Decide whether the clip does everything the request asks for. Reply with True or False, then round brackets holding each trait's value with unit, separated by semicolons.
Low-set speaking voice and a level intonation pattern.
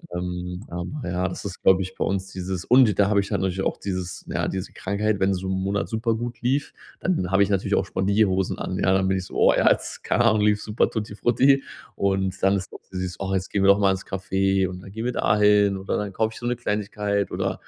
True (100 Hz; 1.9 semitones)